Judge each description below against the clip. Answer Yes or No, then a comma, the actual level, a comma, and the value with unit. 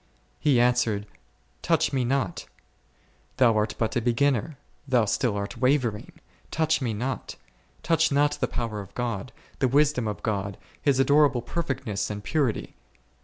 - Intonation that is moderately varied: Yes, average, 4.5 semitones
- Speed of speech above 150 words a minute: No, average, 145 wpm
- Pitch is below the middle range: Yes, low, 125 Hz